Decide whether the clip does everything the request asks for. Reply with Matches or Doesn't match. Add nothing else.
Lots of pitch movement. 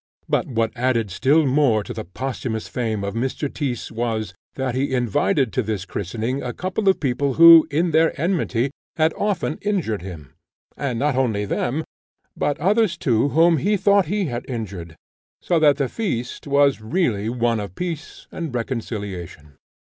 Matches